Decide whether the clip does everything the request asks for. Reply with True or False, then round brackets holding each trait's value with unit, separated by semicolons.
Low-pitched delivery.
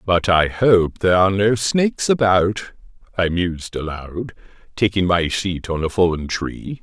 True (95 Hz)